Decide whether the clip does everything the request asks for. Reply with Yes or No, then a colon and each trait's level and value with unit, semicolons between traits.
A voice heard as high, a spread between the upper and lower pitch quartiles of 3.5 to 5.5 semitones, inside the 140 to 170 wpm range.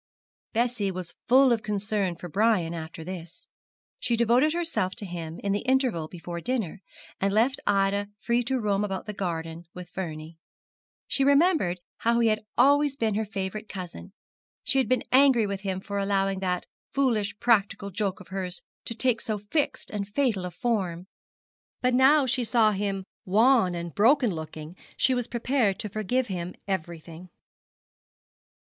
Yes: high, 205 Hz; average, 4.7 semitones; average, 165 wpm